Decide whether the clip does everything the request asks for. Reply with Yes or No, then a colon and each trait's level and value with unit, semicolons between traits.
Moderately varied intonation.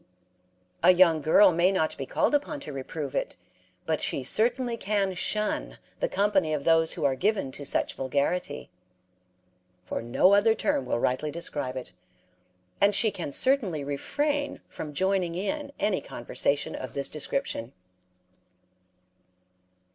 No: wide, 6.6 semitones